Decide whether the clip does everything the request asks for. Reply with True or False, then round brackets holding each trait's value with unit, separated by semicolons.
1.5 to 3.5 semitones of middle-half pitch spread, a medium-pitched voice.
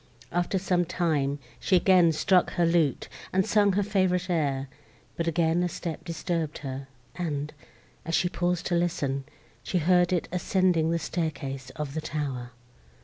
True (3.2 semitones; 170 Hz)